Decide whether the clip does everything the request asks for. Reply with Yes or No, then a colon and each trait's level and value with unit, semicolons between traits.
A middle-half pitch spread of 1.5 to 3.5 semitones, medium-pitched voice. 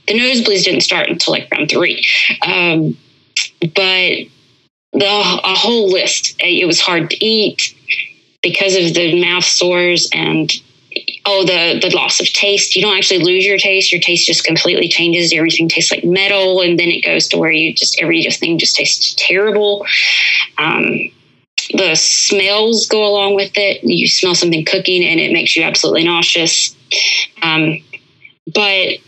Yes: average, 3.1 semitones; medium, 180 Hz